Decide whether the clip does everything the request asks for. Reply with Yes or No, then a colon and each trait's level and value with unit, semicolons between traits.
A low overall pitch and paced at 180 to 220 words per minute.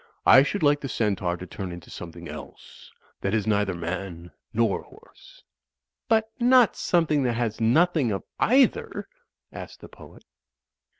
No: low, 115 Hz; average, 145 wpm